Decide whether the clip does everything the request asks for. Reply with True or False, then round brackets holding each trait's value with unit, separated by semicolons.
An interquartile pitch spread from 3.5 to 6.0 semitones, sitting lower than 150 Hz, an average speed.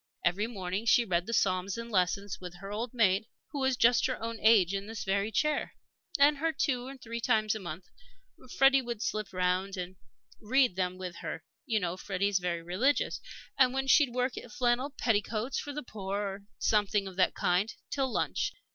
False (4.7 semitones; 215 Hz; 190 wpm)